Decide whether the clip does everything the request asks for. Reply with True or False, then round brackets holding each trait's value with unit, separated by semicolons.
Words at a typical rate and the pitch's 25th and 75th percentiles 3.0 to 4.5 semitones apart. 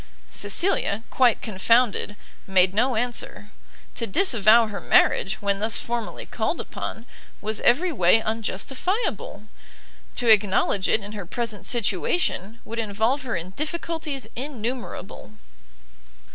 False (115 wpm; 3.7 semitones)